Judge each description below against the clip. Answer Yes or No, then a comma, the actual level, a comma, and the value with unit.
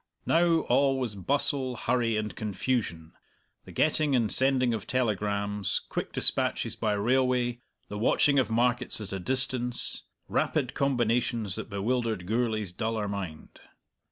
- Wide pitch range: No, average, 3.7 semitones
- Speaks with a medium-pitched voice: No, low, 120 Hz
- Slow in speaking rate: Yes, slow, 130 wpm